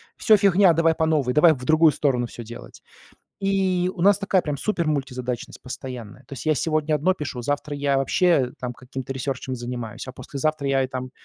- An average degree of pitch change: Yes, average, 4.4 semitones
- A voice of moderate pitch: Yes, medium, 145 Hz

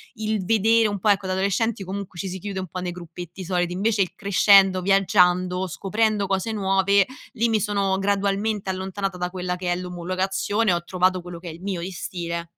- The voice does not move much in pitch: Yes, narrow, 2.0 semitones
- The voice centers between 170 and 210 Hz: Yes, high, 190 Hz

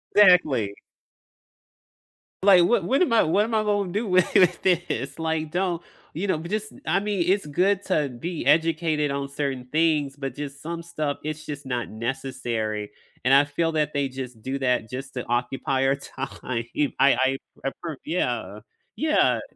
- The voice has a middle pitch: Yes, medium, 150 Hz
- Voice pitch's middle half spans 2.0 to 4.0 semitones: No, average, 4.8 semitones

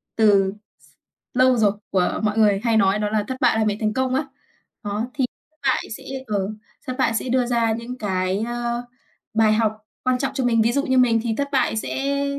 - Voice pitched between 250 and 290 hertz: No, high, 230 Hz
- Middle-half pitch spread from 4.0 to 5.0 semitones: No, average, 3.2 semitones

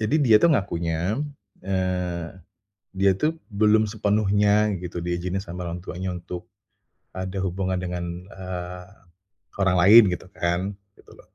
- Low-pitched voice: Yes, very low, 95 Hz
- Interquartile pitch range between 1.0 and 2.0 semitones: No, narrow, 2.6 semitones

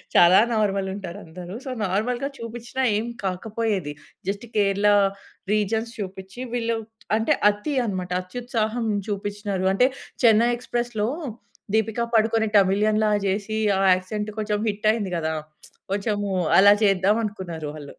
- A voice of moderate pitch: No, high, 210 Hz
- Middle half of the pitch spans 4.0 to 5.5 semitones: No, narrow, 2.6 semitones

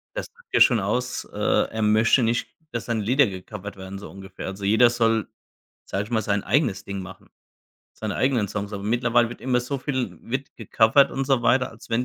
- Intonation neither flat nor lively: Yes, average, 3.6 semitones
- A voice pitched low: Yes, low, 115 Hz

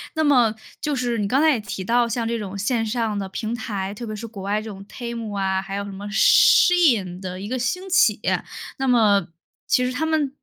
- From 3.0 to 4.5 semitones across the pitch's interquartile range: Yes, average, 4.0 semitones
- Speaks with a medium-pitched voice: No, high, 225 Hz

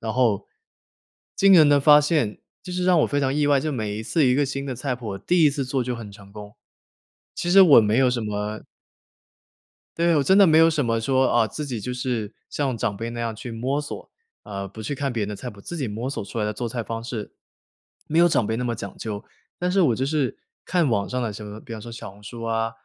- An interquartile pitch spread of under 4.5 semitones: No, average, 4.8 semitones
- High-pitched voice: No, low, 125 Hz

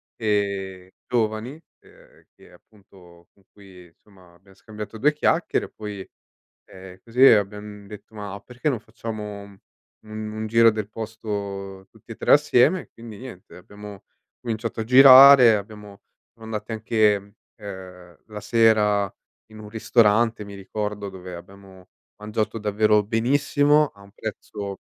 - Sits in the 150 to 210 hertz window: No, low, 105 Hz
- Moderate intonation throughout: No, narrow, 2.2 semitones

